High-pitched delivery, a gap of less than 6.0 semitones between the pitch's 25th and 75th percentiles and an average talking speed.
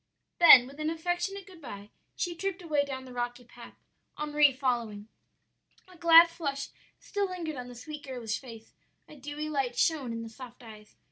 Yes: very high, 280 Hz; average, 5.2 semitones; average, 180 wpm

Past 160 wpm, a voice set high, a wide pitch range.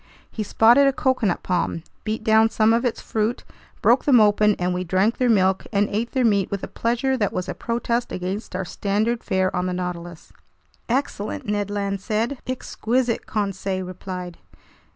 No: average, 175 wpm; high, 210 Hz; average, 3.7 semitones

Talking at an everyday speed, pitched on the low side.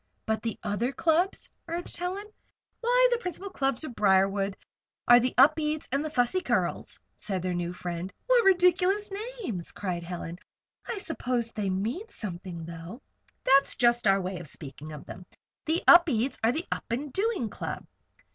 No: average, 165 wpm; high, 240 Hz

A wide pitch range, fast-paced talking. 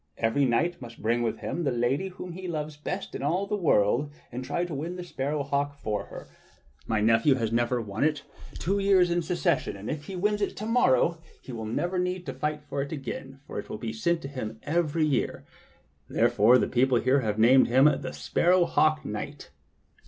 Yes: wide, 6.2 semitones; fast, 220 wpm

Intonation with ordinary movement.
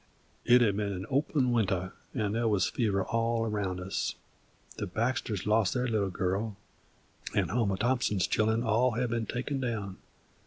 Yes: average, 3.3 semitones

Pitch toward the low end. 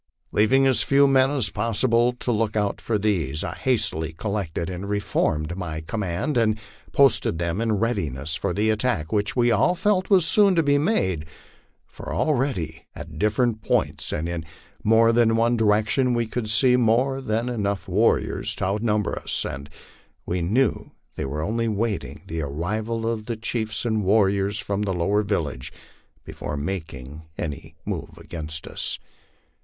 Yes: low, 105 Hz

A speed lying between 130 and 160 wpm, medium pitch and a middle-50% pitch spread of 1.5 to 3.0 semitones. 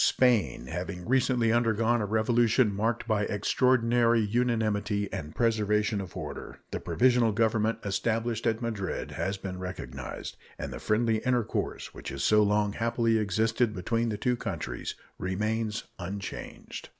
No: average, 140 wpm; low, 110 Hz; narrow, 2.4 semitones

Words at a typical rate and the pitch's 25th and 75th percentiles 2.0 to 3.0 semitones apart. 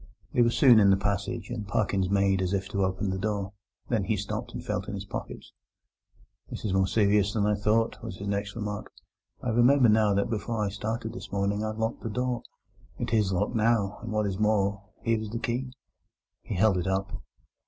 No: fast, 215 wpm; narrow, 2.4 semitones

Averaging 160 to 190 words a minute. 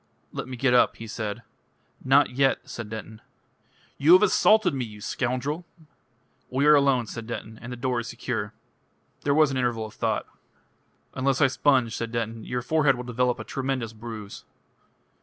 Yes: average, 175 wpm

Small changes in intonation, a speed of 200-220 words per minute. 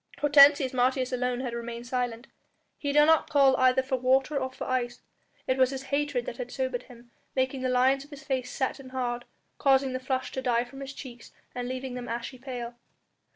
Yes: narrow, 1.5 semitones; fast, 205 wpm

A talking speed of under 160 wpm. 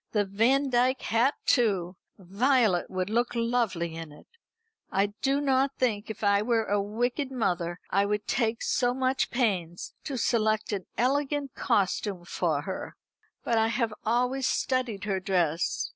Yes: average, 150 wpm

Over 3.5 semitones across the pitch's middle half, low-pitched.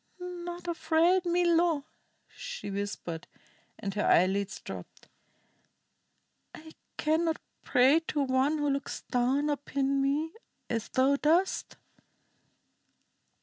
No: average, 4.7 semitones; very high, 290 Hz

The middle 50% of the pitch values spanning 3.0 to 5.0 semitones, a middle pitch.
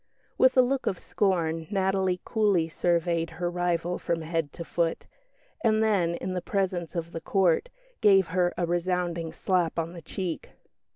No: narrow, 2.4 semitones; medium, 175 Hz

